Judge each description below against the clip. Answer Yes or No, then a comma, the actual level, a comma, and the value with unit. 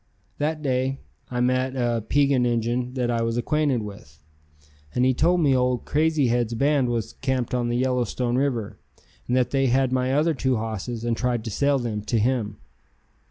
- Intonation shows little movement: Yes, narrow, 2.2 semitones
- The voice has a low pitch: Yes, low, 125 Hz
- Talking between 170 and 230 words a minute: Yes, average, 185 wpm